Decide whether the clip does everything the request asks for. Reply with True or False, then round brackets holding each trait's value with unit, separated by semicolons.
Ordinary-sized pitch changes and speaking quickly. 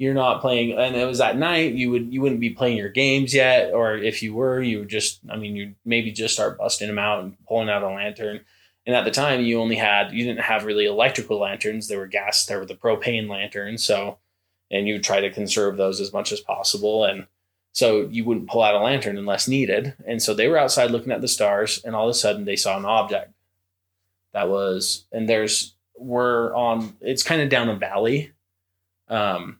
True (3.4 semitones; 225 wpm)